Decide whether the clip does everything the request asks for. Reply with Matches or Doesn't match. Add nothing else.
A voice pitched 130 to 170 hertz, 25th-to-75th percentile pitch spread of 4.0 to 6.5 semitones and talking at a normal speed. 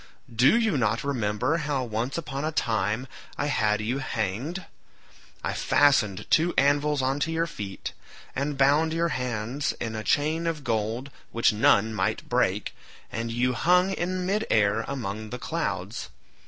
Matches